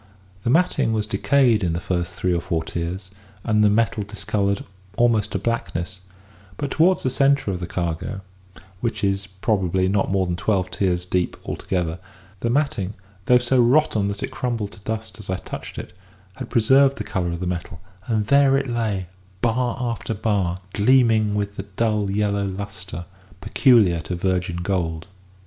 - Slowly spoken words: No, average, 170 wpm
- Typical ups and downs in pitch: Yes, average, 4.1 semitones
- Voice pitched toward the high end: No, low, 100 Hz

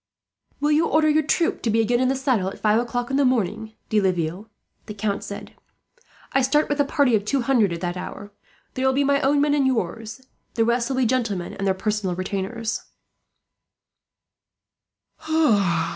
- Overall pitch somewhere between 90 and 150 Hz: No, high, 235 Hz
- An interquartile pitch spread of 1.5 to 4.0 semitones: No, average, 4.8 semitones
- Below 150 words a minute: No, average, 190 wpm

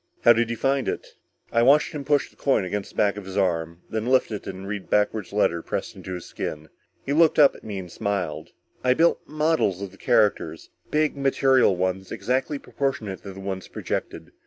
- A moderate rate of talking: No, fast, 210 wpm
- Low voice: Yes, low, 105 Hz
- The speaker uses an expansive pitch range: Yes, wide, 6.1 semitones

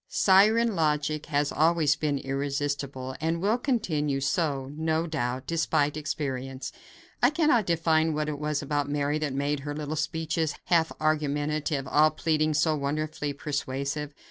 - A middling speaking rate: Yes, average, 145 wpm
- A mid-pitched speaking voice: Yes, medium, 150 Hz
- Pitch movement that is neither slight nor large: No, narrow, 2.1 semitones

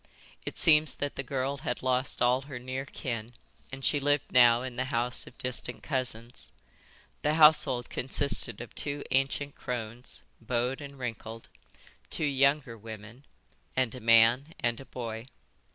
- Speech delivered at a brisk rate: No, average, 150 wpm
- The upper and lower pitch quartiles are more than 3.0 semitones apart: No, average, 2.7 semitones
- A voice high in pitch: No, low, 130 Hz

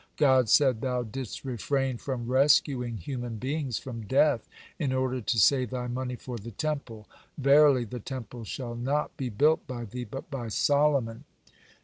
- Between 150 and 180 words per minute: Yes, average, 160 wpm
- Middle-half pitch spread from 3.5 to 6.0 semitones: No, average, 2.7 semitones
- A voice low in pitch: Yes, low, 130 Hz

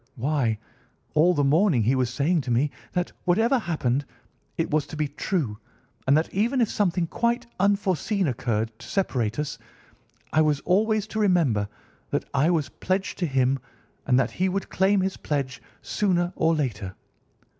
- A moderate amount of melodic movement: No, wide, 6.3 semitones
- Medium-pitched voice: Yes, medium, 155 Hz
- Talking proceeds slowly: No, average, 165 wpm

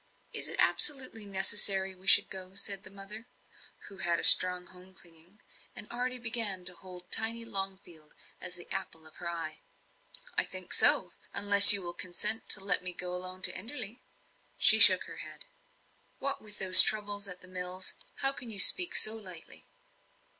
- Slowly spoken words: No, average, 175 wpm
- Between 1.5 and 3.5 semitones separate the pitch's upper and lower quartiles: Yes, average, 2.8 semitones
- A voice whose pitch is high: Yes, high, 195 Hz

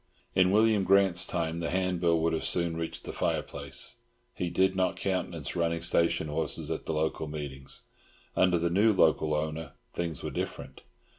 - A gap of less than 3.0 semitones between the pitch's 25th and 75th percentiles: Yes, narrow, 2.5 semitones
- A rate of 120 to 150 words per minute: No, average, 165 wpm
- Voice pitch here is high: No, very low, 85 Hz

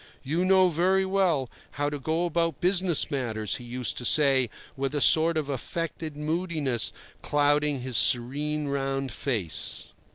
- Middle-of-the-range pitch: Yes, medium, 145 Hz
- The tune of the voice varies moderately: Yes, average, 3.9 semitones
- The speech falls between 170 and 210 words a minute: No, average, 150 wpm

